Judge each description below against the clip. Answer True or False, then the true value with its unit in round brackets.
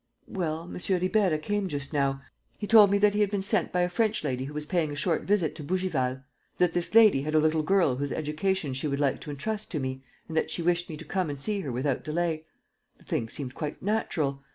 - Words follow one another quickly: True (245 wpm)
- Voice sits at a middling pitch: True (160 Hz)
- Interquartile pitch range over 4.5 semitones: True (5.0 semitones)